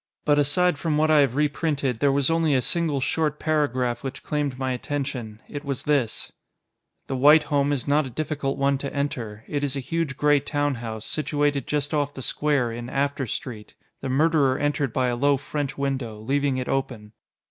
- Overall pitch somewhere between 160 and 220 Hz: No, medium, 140 Hz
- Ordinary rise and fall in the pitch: No, narrow, 2.2 semitones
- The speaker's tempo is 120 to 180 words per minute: No, average, 195 wpm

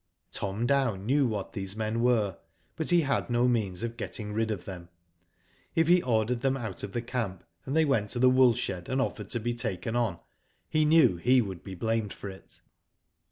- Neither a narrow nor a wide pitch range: Yes, average, 4.4 semitones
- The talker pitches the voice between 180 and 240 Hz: No, low, 115 Hz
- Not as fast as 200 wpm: No, fast, 205 wpm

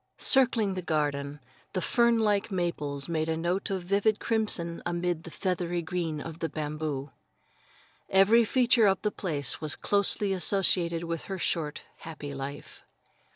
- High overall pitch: No, medium, 175 Hz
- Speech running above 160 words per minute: No, average, 150 wpm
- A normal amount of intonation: Yes, average, 4.2 semitones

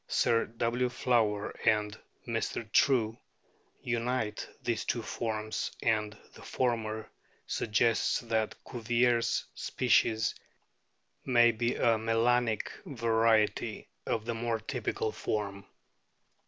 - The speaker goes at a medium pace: No, slow, 100 wpm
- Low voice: Yes, low, 115 Hz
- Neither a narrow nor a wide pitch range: No, narrow, 1.6 semitones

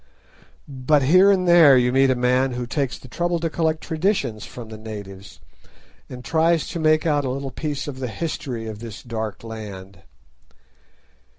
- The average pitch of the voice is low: Yes, low, 130 Hz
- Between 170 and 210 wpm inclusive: Yes, average, 175 wpm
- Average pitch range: No, wide, 5.7 semitones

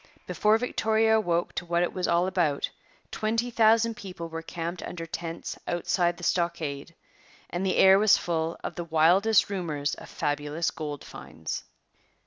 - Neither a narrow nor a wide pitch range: Yes, average, 3.4 semitones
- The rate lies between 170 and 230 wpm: No, average, 155 wpm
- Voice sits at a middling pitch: Yes, medium, 175 Hz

